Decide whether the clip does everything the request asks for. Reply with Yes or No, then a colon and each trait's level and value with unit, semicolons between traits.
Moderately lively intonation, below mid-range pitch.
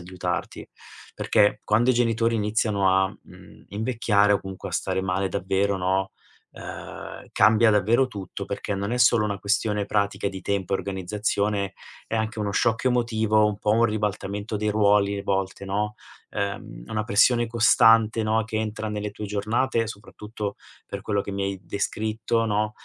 No: narrow, 1.9 semitones; low, 105 Hz